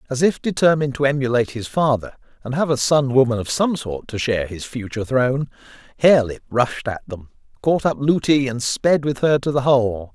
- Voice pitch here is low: Yes, low, 130 Hz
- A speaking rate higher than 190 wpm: Yes, average, 200 wpm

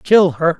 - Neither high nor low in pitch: Yes, medium, 170 Hz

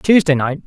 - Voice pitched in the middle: Yes, medium, 155 Hz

